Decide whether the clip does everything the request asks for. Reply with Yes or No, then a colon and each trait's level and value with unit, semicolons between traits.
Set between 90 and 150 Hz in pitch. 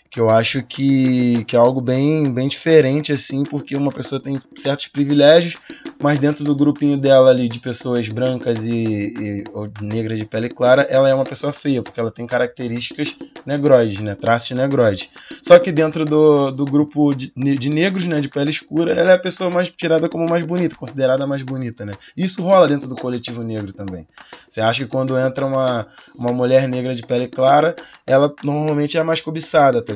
Yes: low, 135 Hz